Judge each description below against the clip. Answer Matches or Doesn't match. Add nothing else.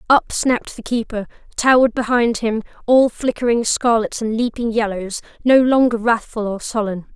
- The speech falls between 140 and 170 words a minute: Matches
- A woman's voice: Matches